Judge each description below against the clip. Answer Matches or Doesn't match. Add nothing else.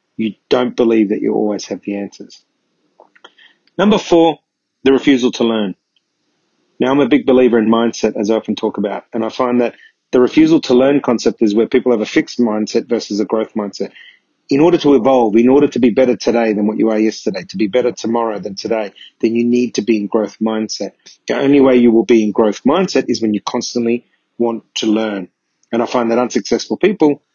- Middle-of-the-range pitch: Doesn't match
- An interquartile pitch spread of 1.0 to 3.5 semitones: Matches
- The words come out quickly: Matches